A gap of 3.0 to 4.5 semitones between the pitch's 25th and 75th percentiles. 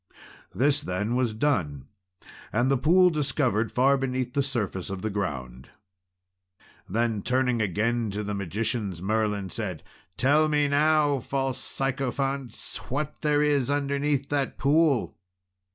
No: average, 5.1 semitones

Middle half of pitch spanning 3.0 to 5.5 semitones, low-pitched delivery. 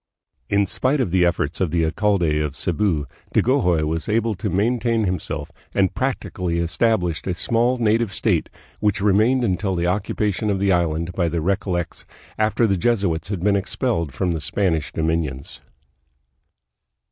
Yes: average, 4.2 semitones; very low, 95 Hz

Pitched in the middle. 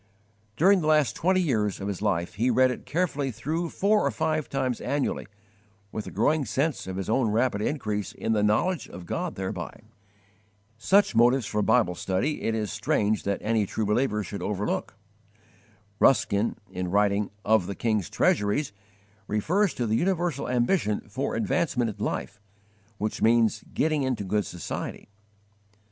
No: low, 115 Hz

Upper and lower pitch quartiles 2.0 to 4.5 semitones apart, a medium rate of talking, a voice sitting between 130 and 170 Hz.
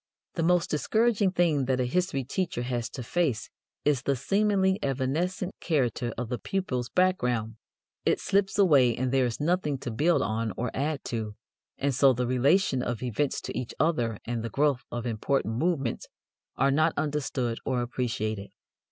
No: wide, 5.6 semitones; average, 170 wpm; low, 135 Hz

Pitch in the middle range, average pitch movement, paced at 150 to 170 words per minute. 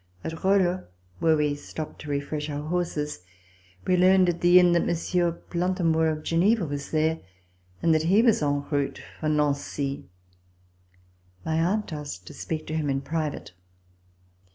Yes: medium, 160 Hz; average, 3.1 semitones; average, 155 wpm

